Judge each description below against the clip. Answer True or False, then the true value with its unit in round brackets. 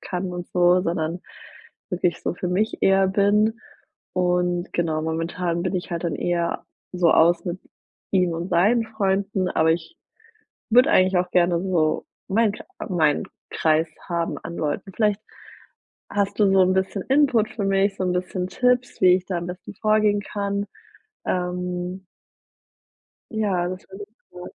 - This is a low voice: False (185 Hz)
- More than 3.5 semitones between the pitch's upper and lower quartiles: False (2.4 semitones)